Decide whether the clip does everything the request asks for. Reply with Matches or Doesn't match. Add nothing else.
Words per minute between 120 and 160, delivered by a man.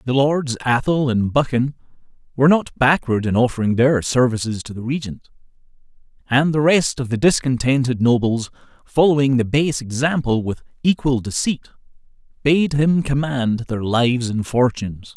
Matches